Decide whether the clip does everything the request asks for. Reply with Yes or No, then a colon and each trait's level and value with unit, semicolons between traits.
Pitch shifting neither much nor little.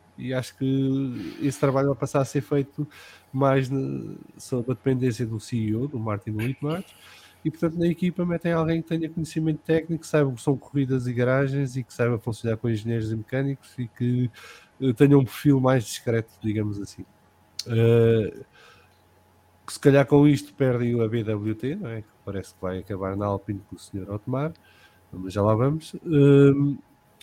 Yes: average, 4.7 semitones